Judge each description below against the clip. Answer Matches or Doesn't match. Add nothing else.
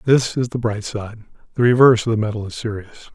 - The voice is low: Matches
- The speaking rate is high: Matches